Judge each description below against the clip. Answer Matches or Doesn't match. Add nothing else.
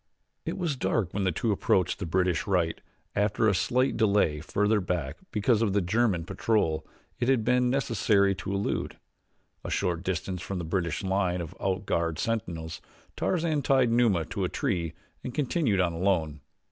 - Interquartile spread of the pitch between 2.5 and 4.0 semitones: Doesn't match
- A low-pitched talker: Matches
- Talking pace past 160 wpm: Matches